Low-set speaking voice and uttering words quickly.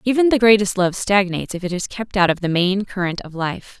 No: high, 195 Hz; fast, 255 wpm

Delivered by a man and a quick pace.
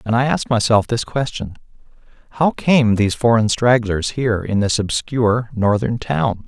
No: male; average, 155 wpm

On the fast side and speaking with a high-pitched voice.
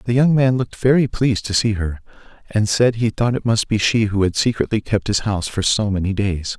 No: fast, 245 wpm; low, 110 Hz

